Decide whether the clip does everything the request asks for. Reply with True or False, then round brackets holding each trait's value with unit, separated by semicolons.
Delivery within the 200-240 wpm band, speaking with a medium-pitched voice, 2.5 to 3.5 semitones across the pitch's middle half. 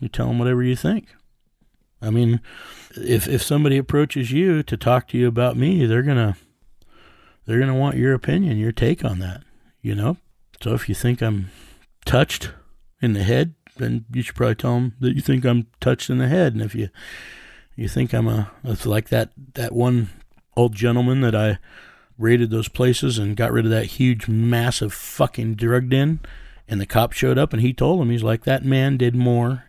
False (205 wpm; 120 Hz; 2.9 semitones)